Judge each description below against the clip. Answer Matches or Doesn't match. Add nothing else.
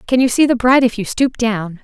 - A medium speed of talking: Doesn't match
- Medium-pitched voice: Doesn't match